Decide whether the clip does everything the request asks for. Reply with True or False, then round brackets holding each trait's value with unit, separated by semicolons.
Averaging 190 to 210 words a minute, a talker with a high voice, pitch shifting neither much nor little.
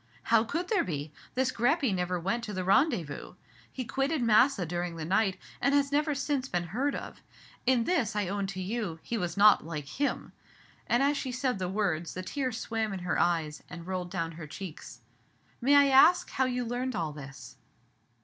False (200 wpm; 210 Hz; 6.7 semitones)